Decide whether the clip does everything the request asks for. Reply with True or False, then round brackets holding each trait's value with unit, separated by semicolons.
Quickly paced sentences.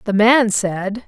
False (165 wpm)